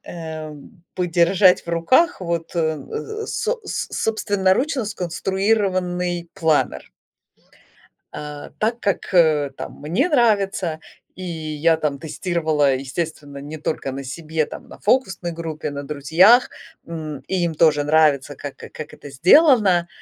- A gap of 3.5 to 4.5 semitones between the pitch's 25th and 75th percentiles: Yes, average, 4.1 semitones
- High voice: No, medium, 170 Hz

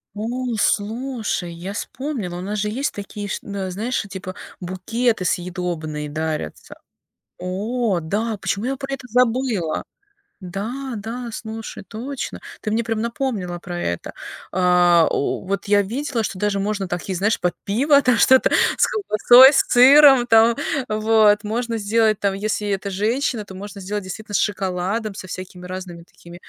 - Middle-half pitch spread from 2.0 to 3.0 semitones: No, average, 4.1 semitones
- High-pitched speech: Yes, high, 210 Hz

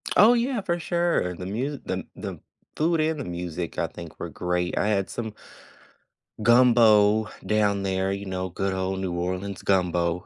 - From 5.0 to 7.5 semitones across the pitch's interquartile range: Yes, wide, 5.5 semitones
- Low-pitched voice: Yes, low, 100 Hz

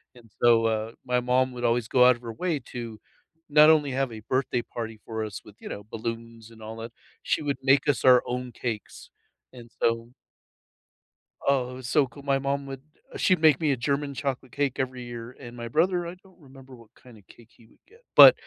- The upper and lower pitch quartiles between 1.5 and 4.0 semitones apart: Yes, average, 3.2 semitones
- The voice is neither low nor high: No, low, 125 Hz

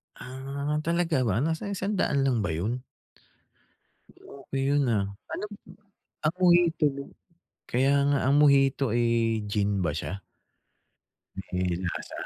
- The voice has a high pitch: No, low, 135 Hz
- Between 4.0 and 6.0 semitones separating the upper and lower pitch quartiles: Yes, average, 5.0 semitones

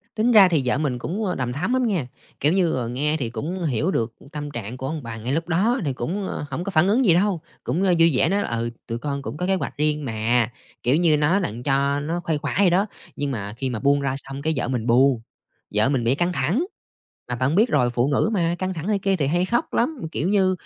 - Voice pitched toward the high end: No, medium, 150 Hz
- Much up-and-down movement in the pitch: Yes, wide, 6.4 semitones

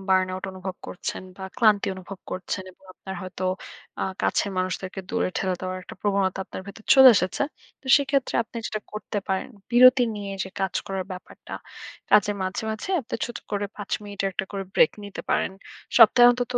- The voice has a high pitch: Yes, high, 200 Hz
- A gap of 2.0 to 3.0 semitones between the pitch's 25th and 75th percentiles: Yes, average, 2.7 semitones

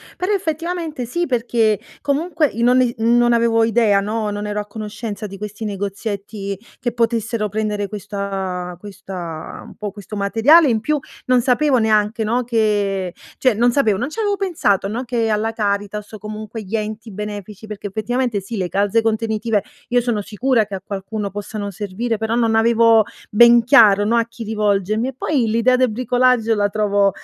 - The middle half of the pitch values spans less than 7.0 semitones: Yes, average, 2.7 semitones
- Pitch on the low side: No, high, 220 Hz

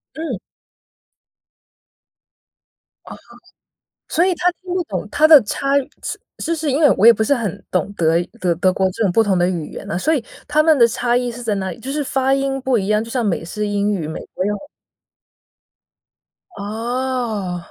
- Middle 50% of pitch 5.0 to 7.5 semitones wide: Yes, wide, 5.5 semitones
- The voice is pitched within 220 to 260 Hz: Yes, high, 230 Hz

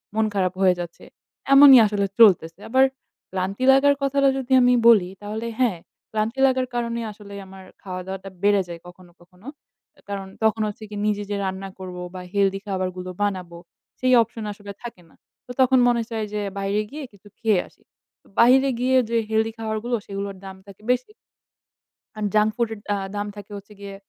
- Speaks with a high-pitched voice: Yes, high, 205 Hz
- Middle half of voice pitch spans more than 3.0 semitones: Yes, average, 3.4 semitones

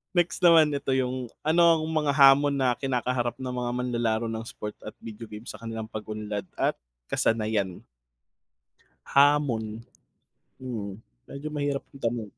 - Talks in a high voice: No, low, 125 Hz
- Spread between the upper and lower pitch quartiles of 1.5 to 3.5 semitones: No, average, 4.1 semitones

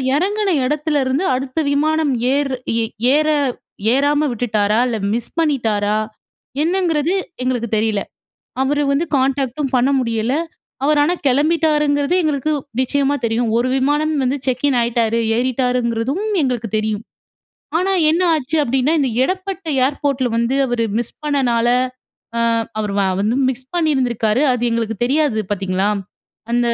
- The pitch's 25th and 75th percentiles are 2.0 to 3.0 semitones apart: No, average, 4.1 semitones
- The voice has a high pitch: Yes, very high, 265 Hz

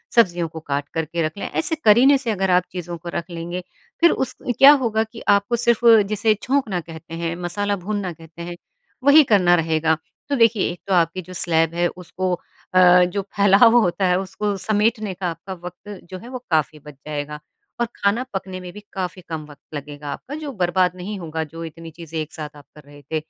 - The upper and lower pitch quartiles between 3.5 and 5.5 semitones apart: Yes, average, 4.1 semitones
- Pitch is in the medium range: Yes, medium, 180 Hz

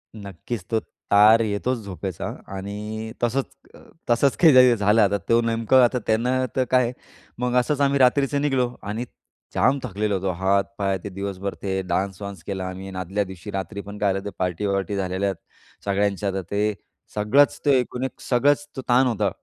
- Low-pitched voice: Yes, low, 105 Hz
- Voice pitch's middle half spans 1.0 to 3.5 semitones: No, average, 4.2 semitones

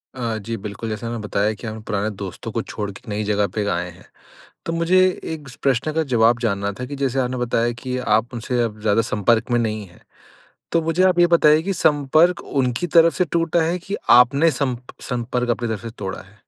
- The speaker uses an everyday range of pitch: No, wide, 5.9 semitones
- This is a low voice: Yes, low, 120 Hz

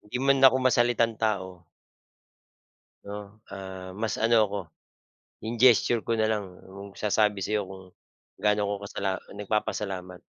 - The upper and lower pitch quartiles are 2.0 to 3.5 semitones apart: Yes, narrow, 2.5 semitones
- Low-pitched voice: Yes, low, 105 Hz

